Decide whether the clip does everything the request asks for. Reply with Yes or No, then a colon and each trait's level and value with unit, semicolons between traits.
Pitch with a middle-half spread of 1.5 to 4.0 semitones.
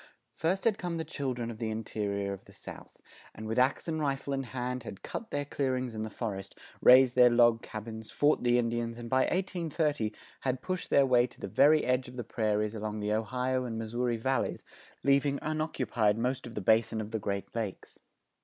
Yes: average, 3.6 semitones